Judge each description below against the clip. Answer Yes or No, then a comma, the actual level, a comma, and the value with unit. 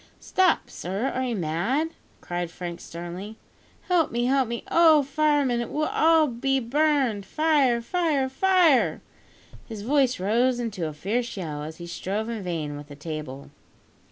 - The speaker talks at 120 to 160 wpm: Yes, average, 155 wpm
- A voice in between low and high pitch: No, high, 235 Hz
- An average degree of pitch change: No, wide, 8.4 semitones